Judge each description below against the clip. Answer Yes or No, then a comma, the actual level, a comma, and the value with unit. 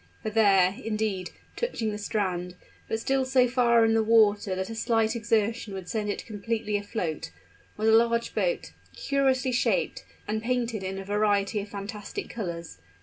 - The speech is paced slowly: No, average, 165 wpm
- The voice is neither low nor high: No, high, 220 Hz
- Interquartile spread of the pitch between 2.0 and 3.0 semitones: Yes, narrow, 2.5 semitones